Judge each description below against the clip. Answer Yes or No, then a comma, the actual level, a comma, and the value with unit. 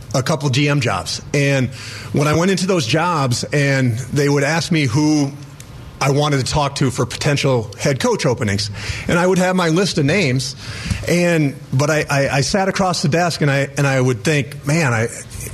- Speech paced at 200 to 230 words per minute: Yes, fast, 205 wpm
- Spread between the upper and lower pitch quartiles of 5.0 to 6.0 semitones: No, average, 3.5 semitones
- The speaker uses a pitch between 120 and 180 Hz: Yes, medium, 140 Hz